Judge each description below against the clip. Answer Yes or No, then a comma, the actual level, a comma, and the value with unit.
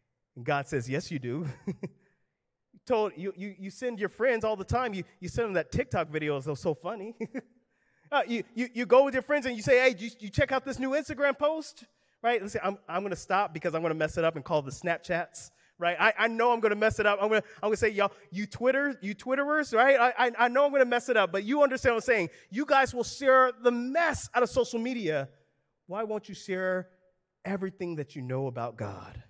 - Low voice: No, high, 210 Hz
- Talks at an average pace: No, fast, 240 wpm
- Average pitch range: No, wide, 6.3 semitones